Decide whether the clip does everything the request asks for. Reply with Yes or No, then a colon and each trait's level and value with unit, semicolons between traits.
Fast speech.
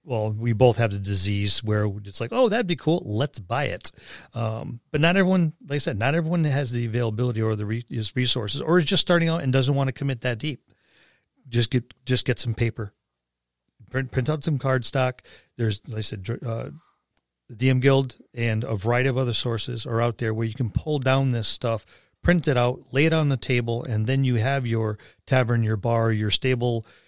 Yes: fast, 215 wpm